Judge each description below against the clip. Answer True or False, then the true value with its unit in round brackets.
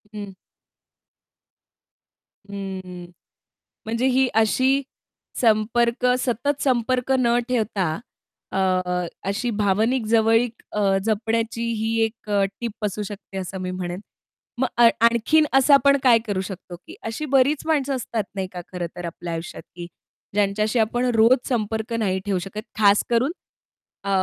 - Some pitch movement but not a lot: True (3.8 semitones)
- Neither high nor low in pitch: False (220 Hz)